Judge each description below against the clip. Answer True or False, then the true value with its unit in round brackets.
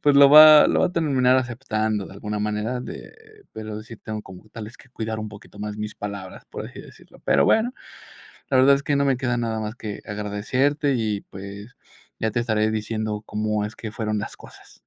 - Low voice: True (110 Hz)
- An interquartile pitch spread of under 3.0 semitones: False (3.3 semitones)